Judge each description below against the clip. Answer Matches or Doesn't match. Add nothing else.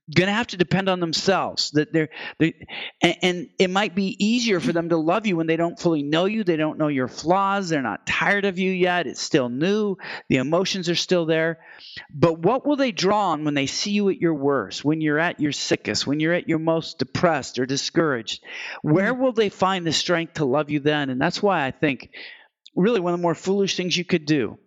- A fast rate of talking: Matches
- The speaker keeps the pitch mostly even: Doesn't match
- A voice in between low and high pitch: Matches